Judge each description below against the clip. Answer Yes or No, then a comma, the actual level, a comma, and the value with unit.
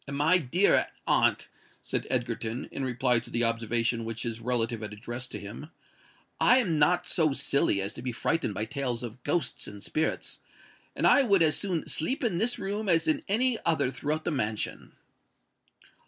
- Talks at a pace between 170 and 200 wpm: Yes, average, 180 wpm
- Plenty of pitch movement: Yes, wide, 6.3 semitones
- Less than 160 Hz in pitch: Yes, low, 135 Hz